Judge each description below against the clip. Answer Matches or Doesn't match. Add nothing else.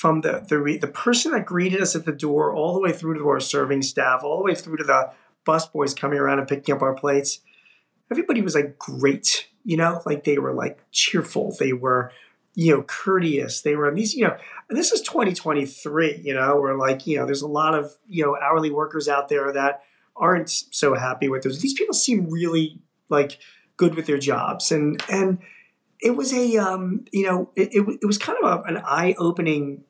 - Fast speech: Matches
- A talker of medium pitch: Matches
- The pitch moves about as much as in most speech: Matches